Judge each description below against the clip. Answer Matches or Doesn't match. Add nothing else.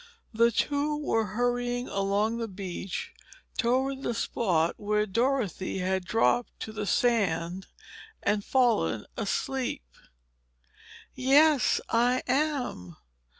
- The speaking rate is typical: Doesn't match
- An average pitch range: Matches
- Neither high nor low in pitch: Doesn't match